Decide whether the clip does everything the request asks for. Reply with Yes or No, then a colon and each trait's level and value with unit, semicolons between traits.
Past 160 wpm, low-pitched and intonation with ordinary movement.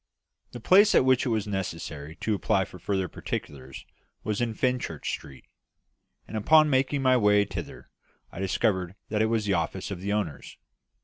Yes: average, 175 wpm; low, 105 Hz; average, 4.7 semitones